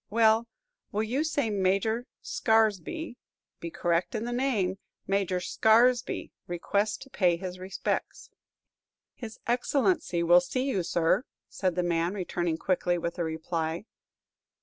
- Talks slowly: Yes, slow, 130 wpm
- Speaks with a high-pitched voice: Yes, high, 195 Hz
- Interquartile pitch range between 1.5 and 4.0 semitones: No, average, 4.9 semitones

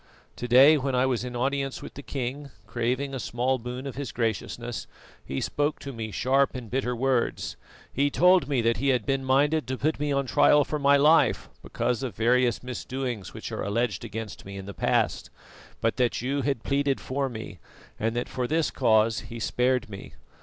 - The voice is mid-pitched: No, low, 130 Hz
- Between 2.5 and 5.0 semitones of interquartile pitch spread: Yes, average, 2.8 semitones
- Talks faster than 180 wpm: Yes, average, 200 wpm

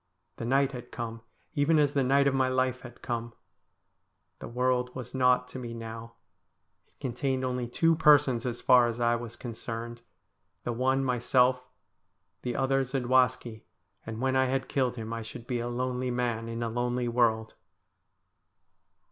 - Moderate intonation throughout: No, narrow, 1.8 semitones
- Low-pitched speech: Yes, low, 125 Hz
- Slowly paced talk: No, average, 165 wpm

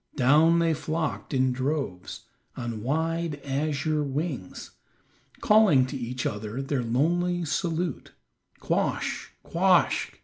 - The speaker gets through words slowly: Yes, slow, 105 wpm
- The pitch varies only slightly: No, average, 4.3 semitones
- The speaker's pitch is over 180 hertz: No, medium, 145 Hz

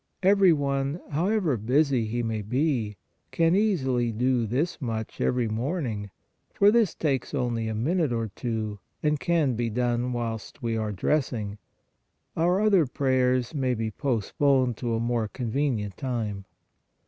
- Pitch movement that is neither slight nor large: Yes, average, 4.8 semitones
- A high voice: No, low, 125 Hz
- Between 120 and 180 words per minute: Yes, average, 150 wpm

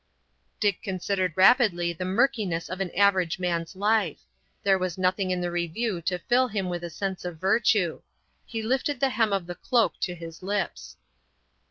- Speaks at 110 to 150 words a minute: No, average, 175 wpm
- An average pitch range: Yes, average, 3.2 semitones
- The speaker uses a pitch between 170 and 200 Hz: Yes, medium, 185 Hz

